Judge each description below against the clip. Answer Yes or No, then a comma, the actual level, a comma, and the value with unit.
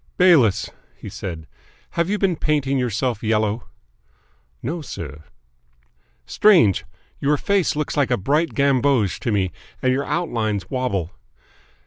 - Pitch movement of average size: No, wide, 6.2 semitones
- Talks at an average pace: No, slow, 120 wpm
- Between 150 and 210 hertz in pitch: No, low, 130 Hz